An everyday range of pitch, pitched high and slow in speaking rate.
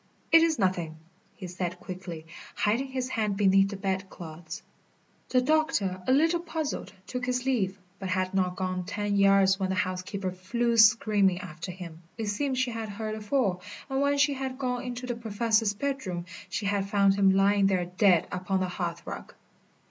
No: average, 4.9 semitones; high, 200 Hz; average, 180 wpm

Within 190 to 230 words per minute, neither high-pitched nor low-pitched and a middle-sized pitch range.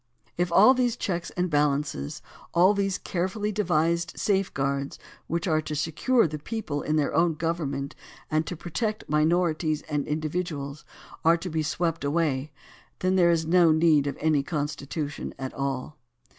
No: average, 155 wpm; medium, 160 Hz; average, 3.2 semitones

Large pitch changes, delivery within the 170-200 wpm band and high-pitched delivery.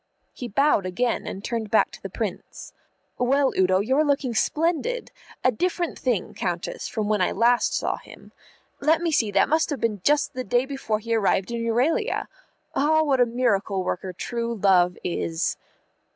Yes: wide, 5.7 semitones; average, 175 wpm; high, 235 Hz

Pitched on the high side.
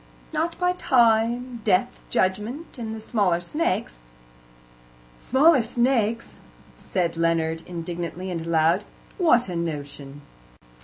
Yes: high, 205 Hz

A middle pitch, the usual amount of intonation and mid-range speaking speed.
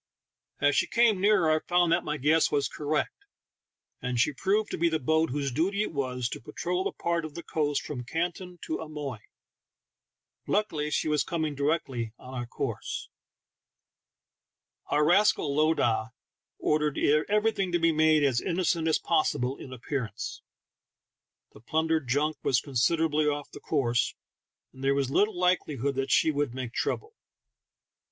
Yes: medium, 150 Hz; average, 3.7 semitones; average, 160 wpm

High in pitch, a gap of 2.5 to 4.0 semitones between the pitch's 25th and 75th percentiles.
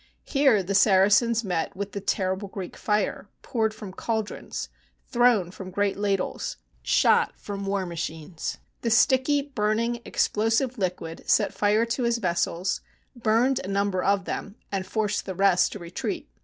Yes: high, 205 Hz; average, 3.3 semitones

